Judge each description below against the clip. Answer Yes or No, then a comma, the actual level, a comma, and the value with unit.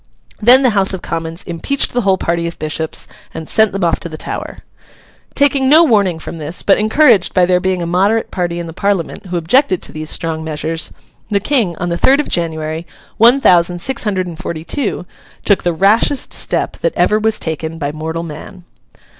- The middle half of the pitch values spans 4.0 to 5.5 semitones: Yes, average, 4.7 semitones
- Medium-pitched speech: Yes, medium, 180 Hz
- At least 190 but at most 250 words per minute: Yes, fast, 205 wpm